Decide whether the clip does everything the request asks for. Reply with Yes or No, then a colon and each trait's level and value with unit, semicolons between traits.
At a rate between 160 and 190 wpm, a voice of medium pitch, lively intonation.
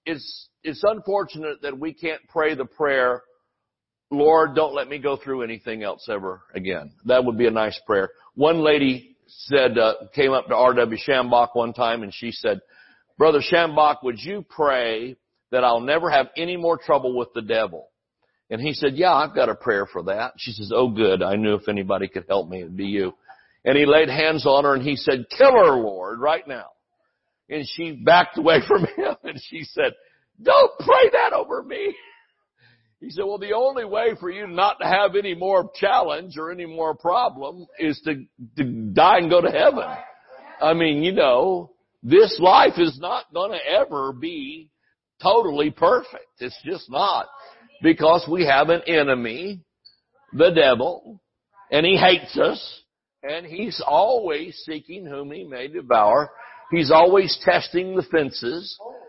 Yes: average, 175 wpm; medium, 160 Hz; wide, 7.3 semitones